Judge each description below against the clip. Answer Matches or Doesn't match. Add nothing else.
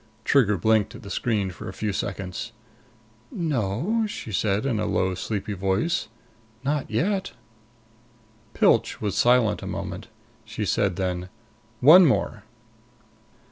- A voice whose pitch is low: Matches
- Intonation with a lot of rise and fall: Matches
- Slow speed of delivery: Matches